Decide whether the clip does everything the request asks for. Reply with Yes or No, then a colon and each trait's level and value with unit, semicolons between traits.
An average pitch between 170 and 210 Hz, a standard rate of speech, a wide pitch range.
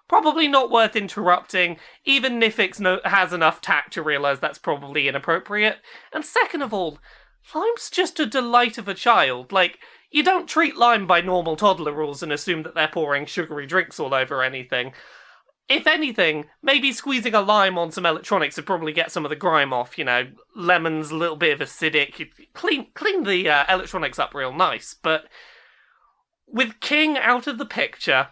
Yes: medium, 185 Hz; average, 180 wpm; wide, 7.8 semitones